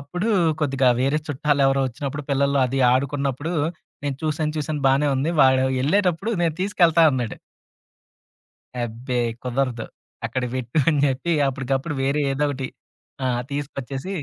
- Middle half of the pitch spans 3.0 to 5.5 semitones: No, narrow, 2.5 semitones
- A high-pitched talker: No, medium, 140 Hz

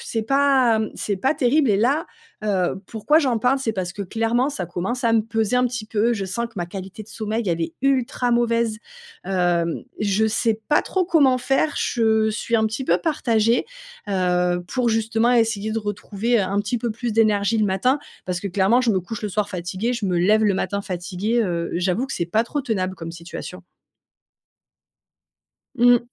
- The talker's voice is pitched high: Yes, high, 220 Hz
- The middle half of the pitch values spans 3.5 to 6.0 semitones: Yes, average, 3.9 semitones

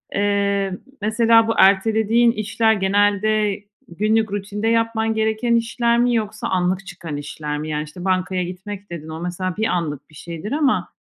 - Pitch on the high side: Yes, high, 205 Hz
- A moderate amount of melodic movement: Yes, average, 3.6 semitones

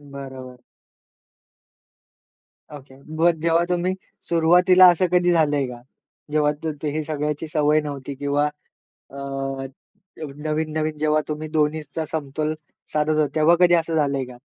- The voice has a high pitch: No, medium, 150 Hz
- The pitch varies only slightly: Yes, narrow, 2.2 semitones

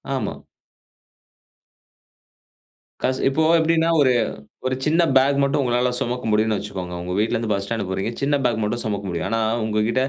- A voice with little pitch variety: No, average, 4.1 semitones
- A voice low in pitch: Yes, low, 115 Hz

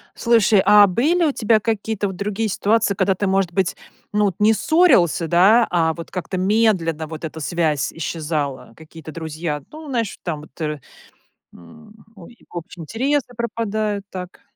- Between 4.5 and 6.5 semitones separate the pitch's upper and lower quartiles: Yes, average, 5.2 semitones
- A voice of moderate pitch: No, high, 195 Hz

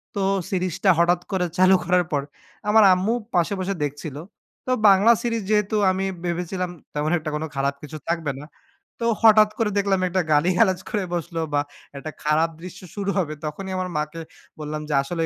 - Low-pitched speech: No, medium, 180 Hz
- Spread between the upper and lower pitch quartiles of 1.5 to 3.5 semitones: No, average, 4.0 semitones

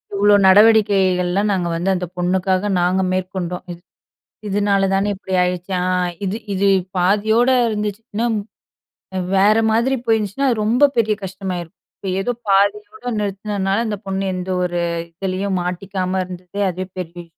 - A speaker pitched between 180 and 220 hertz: Yes, high, 195 Hz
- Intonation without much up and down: Yes, narrow, 2.2 semitones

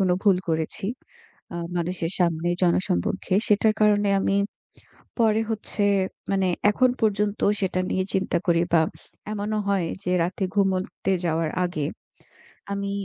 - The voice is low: No, high, 190 Hz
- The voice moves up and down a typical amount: Yes, average, 3.1 semitones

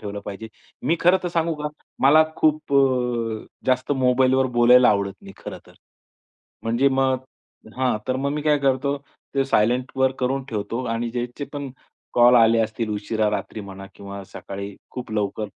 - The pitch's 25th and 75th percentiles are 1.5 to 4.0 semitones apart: Yes, average, 3.7 semitones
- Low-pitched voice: Yes, low, 125 Hz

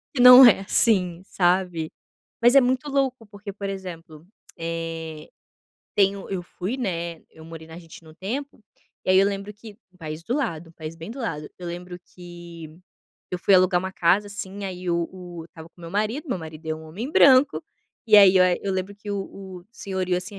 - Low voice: No, medium, 185 Hz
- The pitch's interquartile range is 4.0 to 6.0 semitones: No, average, 3.6 semitones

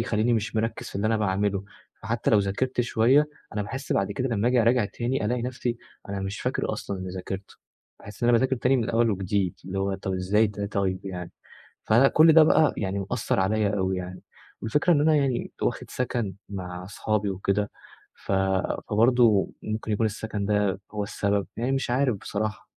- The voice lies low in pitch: Yes, low, 105 Hz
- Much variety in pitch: No, average, 3.5 semitones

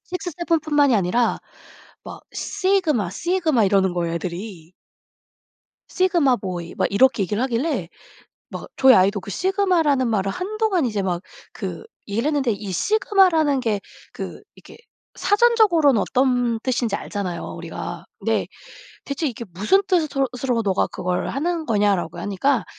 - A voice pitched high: Yes, high, 245 Hz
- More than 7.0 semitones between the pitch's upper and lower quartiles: Yes, wide, 8.6 semitones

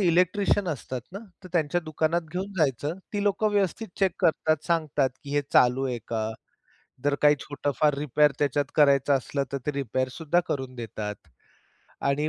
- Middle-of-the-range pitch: Yes, medium, 150 Hz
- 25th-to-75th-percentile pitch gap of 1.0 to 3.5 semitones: No, average, 4.1 semitones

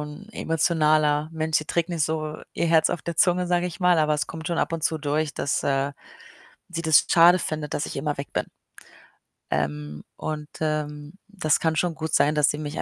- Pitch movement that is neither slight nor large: No, narrow, 2.0 semitones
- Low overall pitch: No, medium, 155 Hz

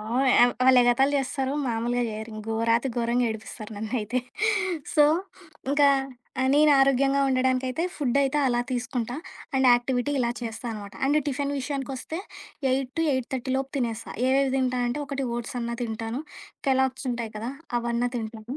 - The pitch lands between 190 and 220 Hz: No, very high, 255 Hz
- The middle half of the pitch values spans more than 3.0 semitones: No, narrow, 2.4 semitones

